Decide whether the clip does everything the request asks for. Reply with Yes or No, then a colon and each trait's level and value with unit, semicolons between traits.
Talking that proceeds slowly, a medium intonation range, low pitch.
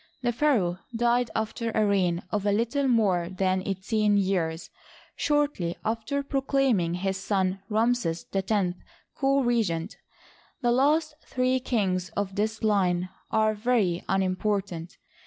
No: slow, 130 wpm; average, 4.5 semitones; high, 210 Hz